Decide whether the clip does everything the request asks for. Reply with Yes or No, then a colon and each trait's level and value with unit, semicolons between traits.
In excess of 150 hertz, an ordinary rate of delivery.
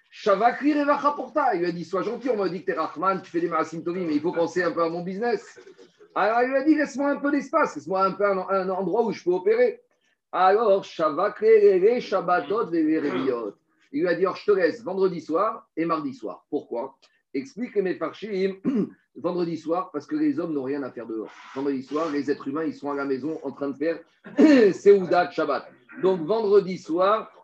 Yes: high, 190 Hz; average, 205 wpm